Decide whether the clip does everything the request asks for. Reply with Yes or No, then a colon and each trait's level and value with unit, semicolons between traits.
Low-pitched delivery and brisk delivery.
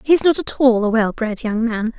No: high, 235 Hz; fast, 305 wpm